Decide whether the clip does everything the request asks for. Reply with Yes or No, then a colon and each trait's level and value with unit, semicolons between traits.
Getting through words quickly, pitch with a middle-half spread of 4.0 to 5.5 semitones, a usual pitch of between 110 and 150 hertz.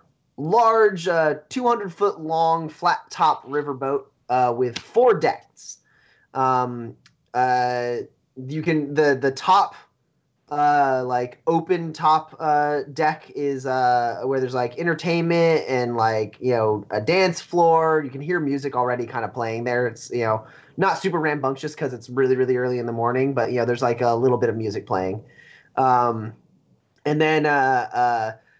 No: average, 160 wpm; average, 4.4 semitones; low, 135 Hz